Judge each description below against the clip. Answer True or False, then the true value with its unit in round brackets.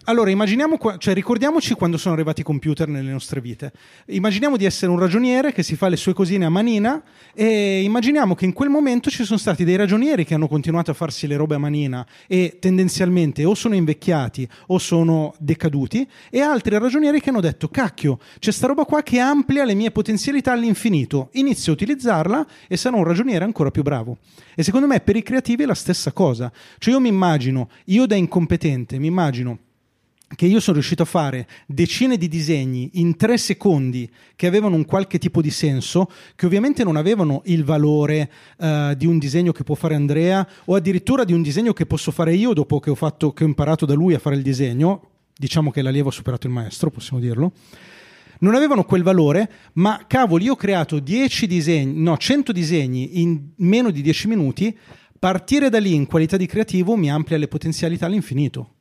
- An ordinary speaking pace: False (195 wpm)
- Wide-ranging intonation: True (6.1 semitones)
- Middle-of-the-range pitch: True (175 Hz)